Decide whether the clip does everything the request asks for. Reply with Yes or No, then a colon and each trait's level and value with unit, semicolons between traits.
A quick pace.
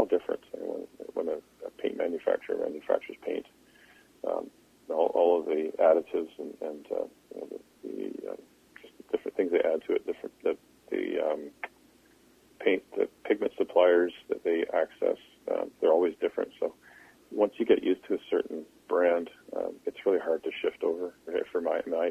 No: average, 185 wpm